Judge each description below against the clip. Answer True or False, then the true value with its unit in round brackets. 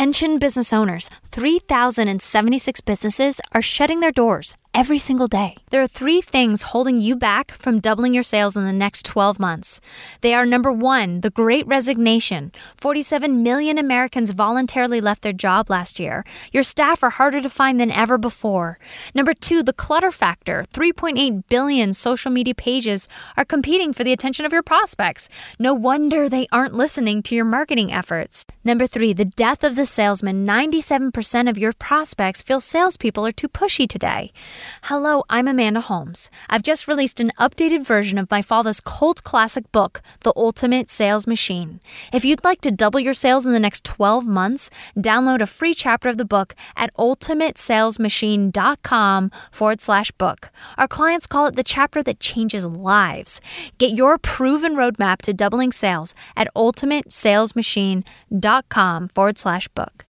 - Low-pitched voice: False (245 Hz)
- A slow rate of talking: False (160 wpm)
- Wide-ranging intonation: False (4.4 semitones)